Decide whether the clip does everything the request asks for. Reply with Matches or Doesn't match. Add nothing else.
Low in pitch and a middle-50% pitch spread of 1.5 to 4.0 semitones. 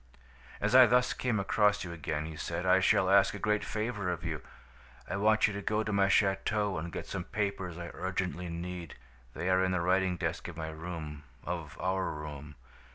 Matches